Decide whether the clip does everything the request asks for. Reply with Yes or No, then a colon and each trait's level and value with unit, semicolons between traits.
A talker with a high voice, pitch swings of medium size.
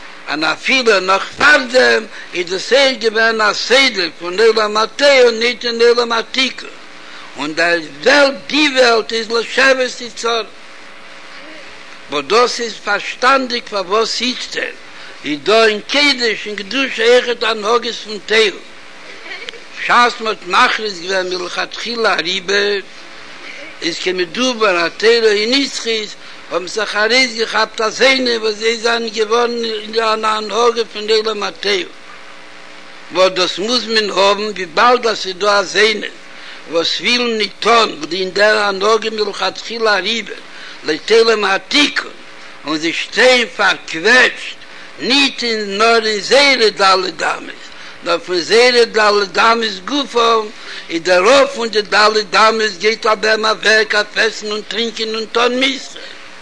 Yes: high, 220 Hz; average, 3.9 semitones